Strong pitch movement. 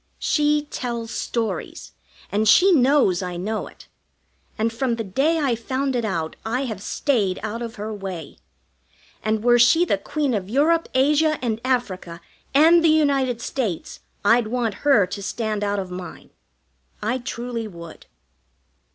No: average, 4.9 semitones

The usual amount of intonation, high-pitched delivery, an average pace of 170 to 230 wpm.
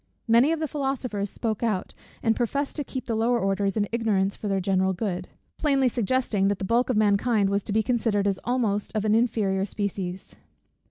Yes: average, 3.5 semitones; high, 215 Hz; average, 200 wpm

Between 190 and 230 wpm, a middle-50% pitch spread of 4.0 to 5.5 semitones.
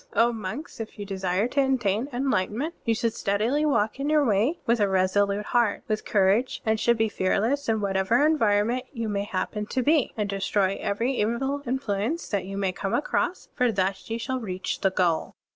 Yes: average, 195 wpm; average, 4.4 semitones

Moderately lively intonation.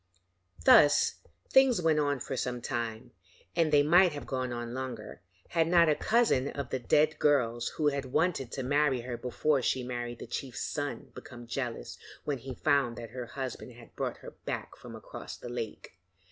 Yes: average, 3.6 semitones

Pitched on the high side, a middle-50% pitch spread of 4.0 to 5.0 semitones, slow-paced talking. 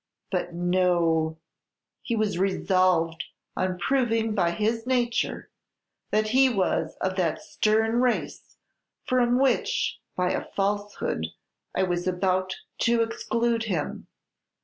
Yes: high, 200 Hz; average, 4.4 semitones; slow, 115 wpm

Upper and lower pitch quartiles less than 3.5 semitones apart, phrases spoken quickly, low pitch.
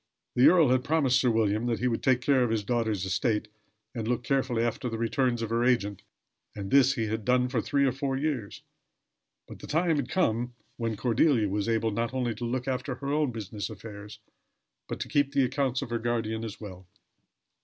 Yes: average, 3.0 semitones; fast, 210 wpm; low, 120 Hz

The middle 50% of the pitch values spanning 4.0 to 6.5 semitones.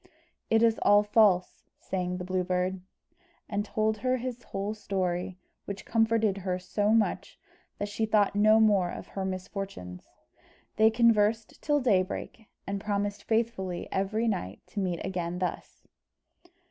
No: average, 3.0 semitones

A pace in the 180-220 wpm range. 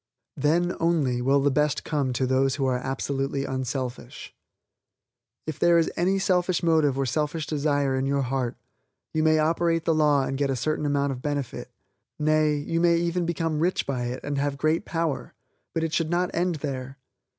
Yes: average, 185 wpm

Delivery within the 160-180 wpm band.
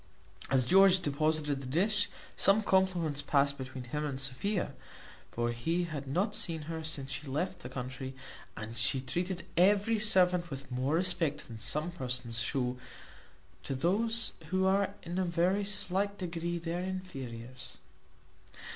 No: average, 145 wpm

